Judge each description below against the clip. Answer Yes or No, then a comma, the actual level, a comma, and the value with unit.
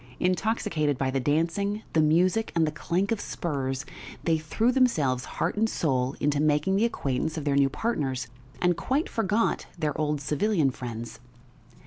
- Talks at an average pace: Yes, average, 160 wpm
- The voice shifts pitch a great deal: Yes, wide, 6.3 semitones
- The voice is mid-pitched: Yes, medium, 155 Hz